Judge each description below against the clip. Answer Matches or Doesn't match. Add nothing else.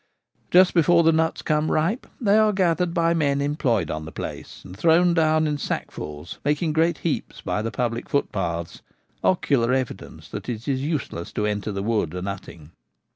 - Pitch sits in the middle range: Matches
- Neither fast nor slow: Matches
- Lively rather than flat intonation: Matches